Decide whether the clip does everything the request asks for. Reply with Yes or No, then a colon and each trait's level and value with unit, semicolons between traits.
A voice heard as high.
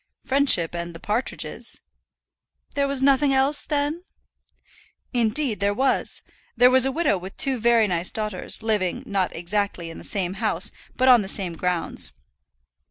Yes: high, 220 Hz